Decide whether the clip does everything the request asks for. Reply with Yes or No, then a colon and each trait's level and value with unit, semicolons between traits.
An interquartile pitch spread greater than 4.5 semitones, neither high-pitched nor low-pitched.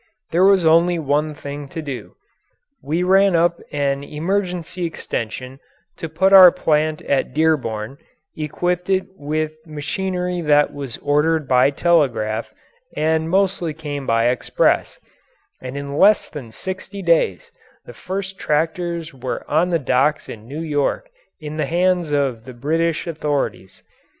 No: average, 3.7 semitones; medium, 155 Hz